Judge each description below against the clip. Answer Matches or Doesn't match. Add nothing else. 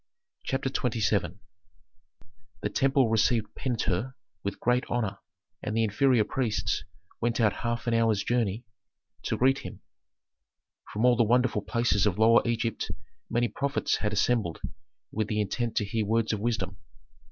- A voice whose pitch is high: Doesn't match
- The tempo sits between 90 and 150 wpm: Matches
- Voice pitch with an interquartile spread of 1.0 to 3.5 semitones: Matches